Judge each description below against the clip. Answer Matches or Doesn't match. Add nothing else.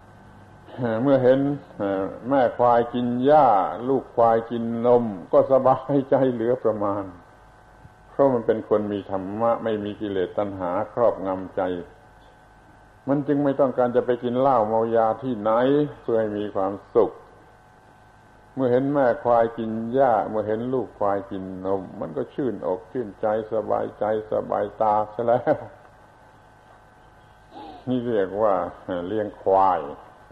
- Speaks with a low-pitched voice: Matches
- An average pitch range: Matches